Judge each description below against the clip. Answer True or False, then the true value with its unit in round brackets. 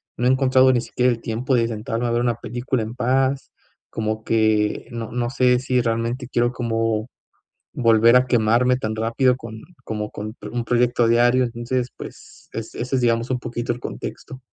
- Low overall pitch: True (120 Hz)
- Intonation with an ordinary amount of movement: False (1.9 semitones)